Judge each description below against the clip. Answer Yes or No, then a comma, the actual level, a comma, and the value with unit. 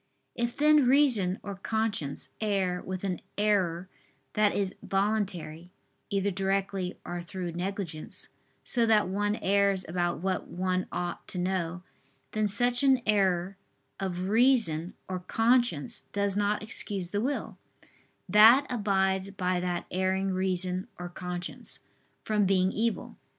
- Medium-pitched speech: No, high, 195 Hz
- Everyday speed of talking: No, slow, 130 wpm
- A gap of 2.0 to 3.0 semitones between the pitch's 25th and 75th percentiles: Yes, average, 2.7 semitones